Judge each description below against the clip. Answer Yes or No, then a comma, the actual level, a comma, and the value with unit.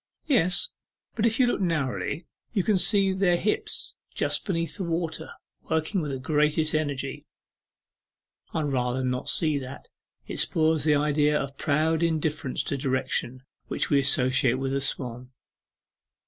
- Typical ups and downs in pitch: Yes, average, 3.8 semitones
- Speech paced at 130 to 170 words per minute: Yes, average, 145 wpm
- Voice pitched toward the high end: No, medium, 150 Hz